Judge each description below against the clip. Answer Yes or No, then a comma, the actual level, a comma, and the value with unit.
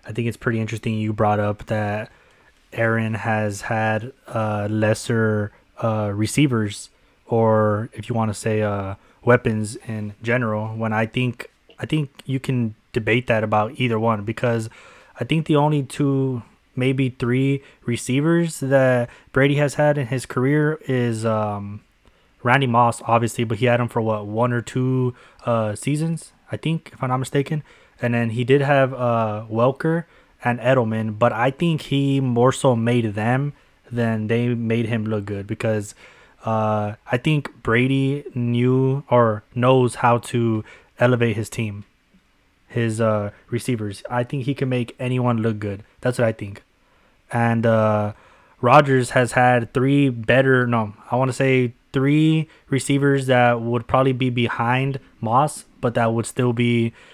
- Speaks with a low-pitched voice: Yes, low, 120 Hz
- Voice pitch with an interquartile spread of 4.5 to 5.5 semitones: No, average, 2.9 semitones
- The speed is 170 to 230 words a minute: No, average, 160 wpm